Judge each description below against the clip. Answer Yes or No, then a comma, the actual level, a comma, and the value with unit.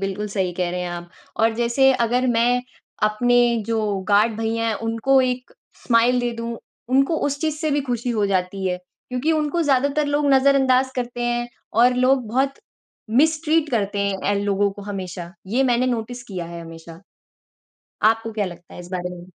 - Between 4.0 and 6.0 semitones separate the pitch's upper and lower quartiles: Yes, average, 4.3 semitones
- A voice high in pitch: Yes, high, 235 Hz